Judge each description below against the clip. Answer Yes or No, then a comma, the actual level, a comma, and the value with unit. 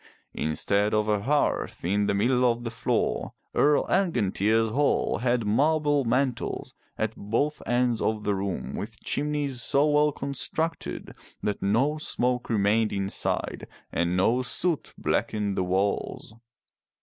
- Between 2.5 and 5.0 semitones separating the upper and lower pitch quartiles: No, wide, 5.4 semitones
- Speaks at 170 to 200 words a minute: No, slow, 135 wpm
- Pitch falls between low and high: No, low, 115 Hz